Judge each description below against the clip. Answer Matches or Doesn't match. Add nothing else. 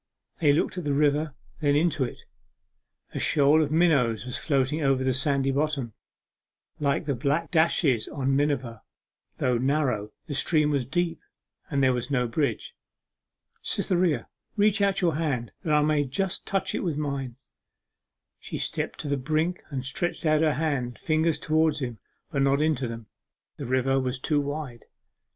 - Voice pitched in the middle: Matches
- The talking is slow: Doesn't match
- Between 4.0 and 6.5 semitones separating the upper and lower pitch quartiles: Doesn't match